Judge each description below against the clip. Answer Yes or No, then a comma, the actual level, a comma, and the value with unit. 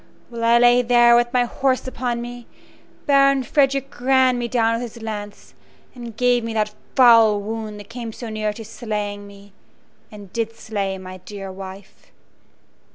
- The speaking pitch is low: No, high, 230 Hz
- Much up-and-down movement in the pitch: No, average, 2.8 semitones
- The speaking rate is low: No, average, 165 wpm